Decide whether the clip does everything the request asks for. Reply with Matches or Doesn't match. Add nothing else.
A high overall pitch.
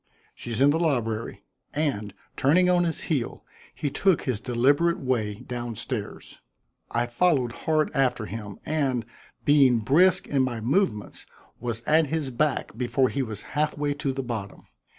Doesn't match